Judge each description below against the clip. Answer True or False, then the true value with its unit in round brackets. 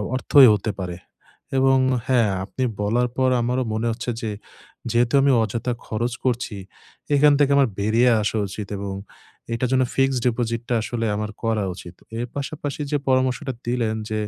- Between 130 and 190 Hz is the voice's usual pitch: False (120 Hz)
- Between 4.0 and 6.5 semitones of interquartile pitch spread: False (3.0 semitones)